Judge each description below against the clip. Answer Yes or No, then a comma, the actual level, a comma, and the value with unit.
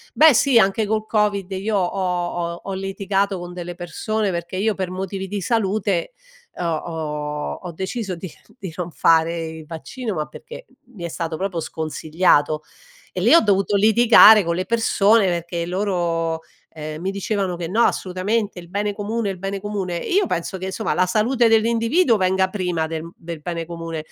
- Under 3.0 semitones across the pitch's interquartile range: No, average, 3.5 semitones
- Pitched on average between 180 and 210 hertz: Yes, medium, 185 Hz